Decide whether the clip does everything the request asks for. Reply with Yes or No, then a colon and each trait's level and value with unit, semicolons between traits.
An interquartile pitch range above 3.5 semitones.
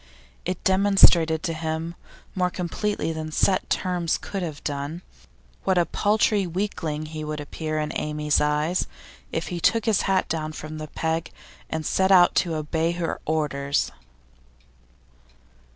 No: average, 2.9 semitones